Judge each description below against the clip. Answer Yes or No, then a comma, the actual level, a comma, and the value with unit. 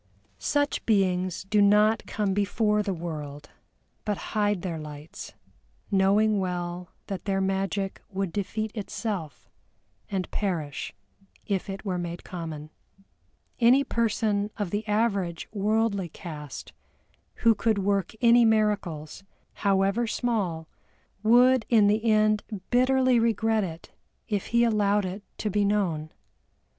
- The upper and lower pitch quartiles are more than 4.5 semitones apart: No, average, 3.2 semitones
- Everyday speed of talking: No, slow, 125 wpm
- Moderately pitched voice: No, high, 200 Hz